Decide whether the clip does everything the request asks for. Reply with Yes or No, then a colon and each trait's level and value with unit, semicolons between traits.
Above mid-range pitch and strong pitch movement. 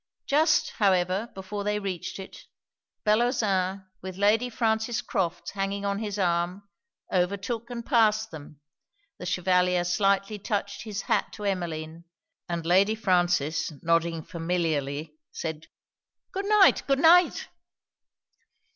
No: high, 195 Hz; average, 3.6 semitones